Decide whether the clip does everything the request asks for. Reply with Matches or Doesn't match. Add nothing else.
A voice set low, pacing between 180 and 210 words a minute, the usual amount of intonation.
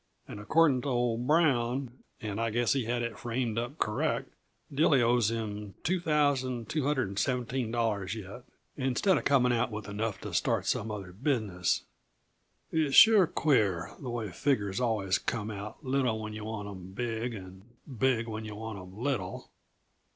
Doesn't match